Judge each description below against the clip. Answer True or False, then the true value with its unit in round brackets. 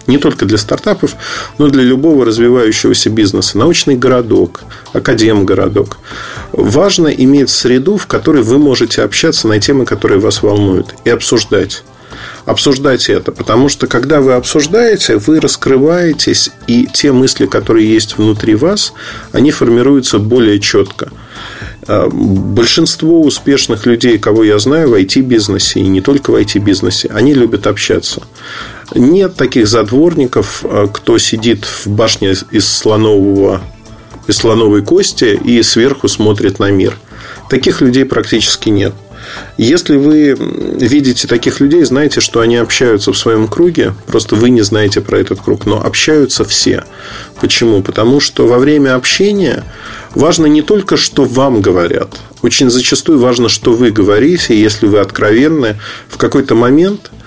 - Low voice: True (125 Hz)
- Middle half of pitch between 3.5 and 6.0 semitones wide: True (5.2 semitones)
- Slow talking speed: False (135 wpm)